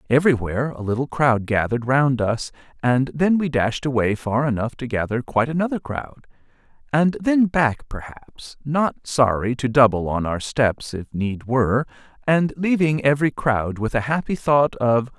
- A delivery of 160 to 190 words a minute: Yes, average, 165 wpm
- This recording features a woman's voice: No, male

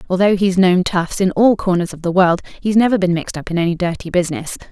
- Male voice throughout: No, female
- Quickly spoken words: Yes, fast, 240 wpm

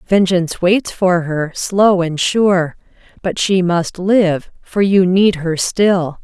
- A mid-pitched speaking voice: Yes, medium, 180 Hz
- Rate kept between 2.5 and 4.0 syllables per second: Yes, 3.3 syllables/s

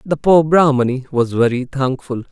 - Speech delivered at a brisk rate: No, average, 155 wpm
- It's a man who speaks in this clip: Yes, male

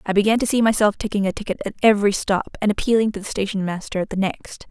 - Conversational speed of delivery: No, fast, 255 wpm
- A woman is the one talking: Yes, female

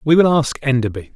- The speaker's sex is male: Yes, male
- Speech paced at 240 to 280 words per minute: No, fast, 205 wpm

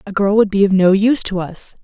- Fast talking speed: Yes, fast, 295 wpm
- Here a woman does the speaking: Yes, female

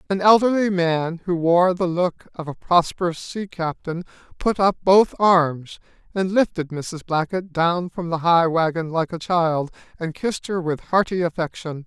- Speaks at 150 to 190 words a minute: Yes, average, 170 wpm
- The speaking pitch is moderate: Yes, medium, 175 Hz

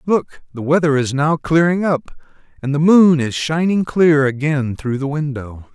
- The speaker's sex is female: No, male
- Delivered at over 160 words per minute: Yes, average, 180 wpm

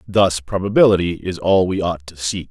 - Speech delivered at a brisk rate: No, average, 190 wpm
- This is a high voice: No, very low, 90 Hz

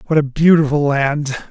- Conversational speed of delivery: Yes, average, 160 wpm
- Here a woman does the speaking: No, male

